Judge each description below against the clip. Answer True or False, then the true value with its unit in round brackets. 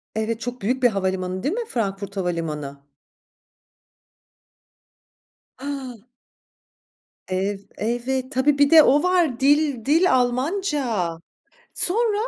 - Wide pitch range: True (6.7 semitones)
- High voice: True (250 Hz)